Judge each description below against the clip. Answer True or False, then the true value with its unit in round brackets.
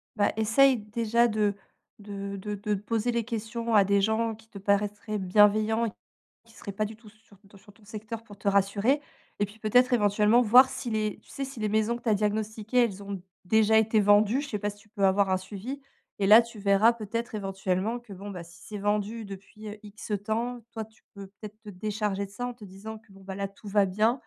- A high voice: True (210 Hz)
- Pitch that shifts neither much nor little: False (2.0 semitones)